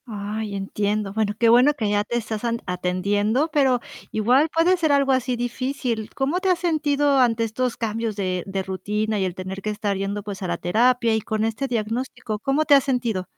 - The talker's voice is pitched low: No, high, 225 Hz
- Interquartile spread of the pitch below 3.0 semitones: No, average, 4.1 semitones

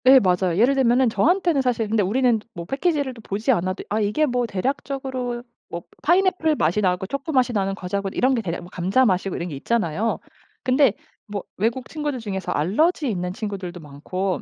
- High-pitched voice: Yes, high, 225 Hz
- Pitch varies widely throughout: Yes, wide, 5.9 semitones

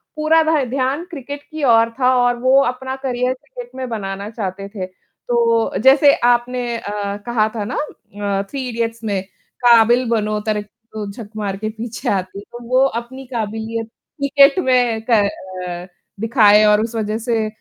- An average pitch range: Yes, average, 3.3 semitones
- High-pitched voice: Yes, high, 230 Hz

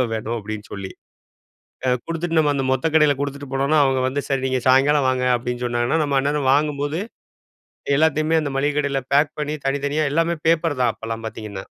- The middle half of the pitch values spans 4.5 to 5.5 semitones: No, average, 2.8 semitones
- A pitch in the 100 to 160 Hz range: Yes, medium, 140 Hz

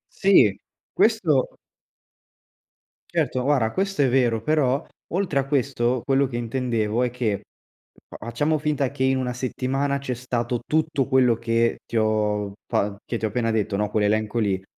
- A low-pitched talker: Yes, low, 125 Hz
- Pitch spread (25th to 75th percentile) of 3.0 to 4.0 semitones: Yes, average, 3.6 semitones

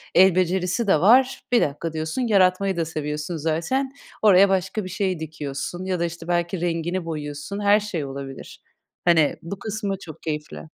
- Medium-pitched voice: Yes, medium, 175 Hz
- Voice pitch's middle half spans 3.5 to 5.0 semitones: Yes, average, 3.8 semitones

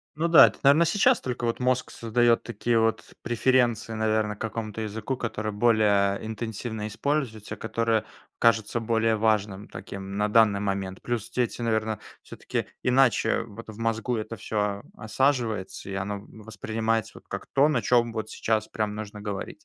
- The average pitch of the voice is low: Yes, low, 110 Hz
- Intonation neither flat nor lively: No, narrow, 2.0 semitones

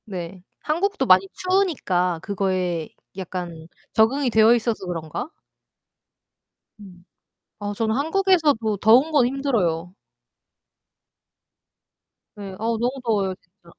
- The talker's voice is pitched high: Yes, high, 210 Hz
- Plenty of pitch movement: Yes, wide, 6.4 semitones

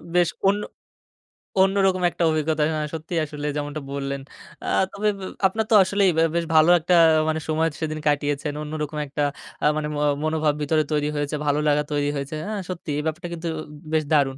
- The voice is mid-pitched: Yes, medium, 155 Hz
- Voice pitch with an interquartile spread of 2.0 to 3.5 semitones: Yes, narrow, 2.5 semitones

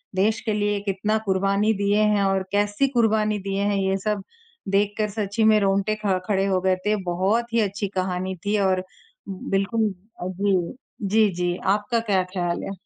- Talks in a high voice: Yes, high, 200 Hz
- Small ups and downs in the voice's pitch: Yes, narrow, 1.8 semitones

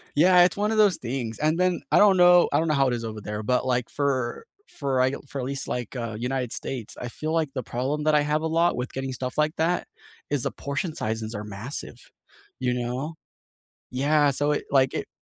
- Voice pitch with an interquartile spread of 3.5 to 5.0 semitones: Yes, average, 4.0 semitones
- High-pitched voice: No, low, 135 Hz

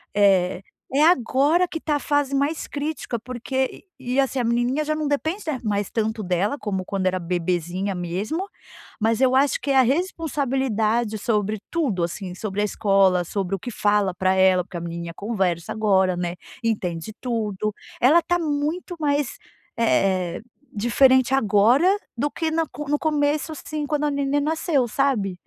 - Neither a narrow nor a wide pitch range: No, wide, 7.0 semitones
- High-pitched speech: Yes, high, 235 Hz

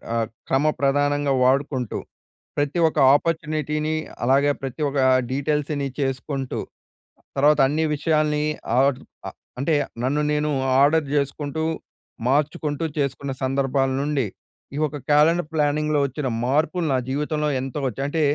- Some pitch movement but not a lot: No, narrow, 1.9 semitones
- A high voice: No, medium, 145 Hz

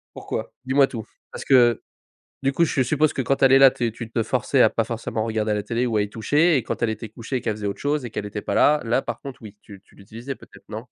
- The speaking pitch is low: Yes, low, 120 Hz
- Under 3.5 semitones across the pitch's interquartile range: No, average, 3.8 semitones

